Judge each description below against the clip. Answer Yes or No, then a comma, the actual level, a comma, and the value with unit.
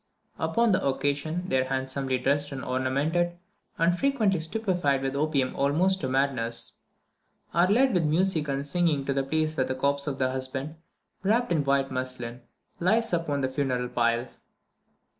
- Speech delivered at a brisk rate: No, average, 160 wpm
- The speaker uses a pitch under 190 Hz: Yes, medium, 140 Hz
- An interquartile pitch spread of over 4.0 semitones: Yes, average, 4.7 semitones